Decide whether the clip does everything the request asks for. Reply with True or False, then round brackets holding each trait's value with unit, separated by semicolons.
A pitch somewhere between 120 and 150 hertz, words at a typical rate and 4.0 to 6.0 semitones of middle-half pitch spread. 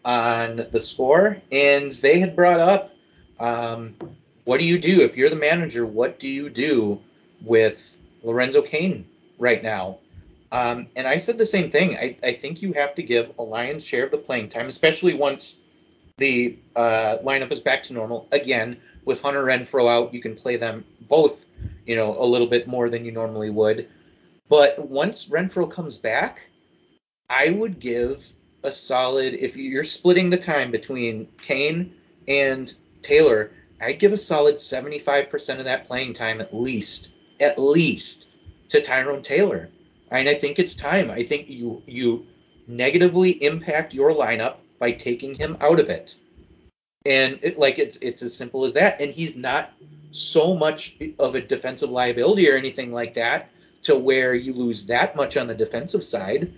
True (135 Hz; 175 wpm; 5.1 semitones)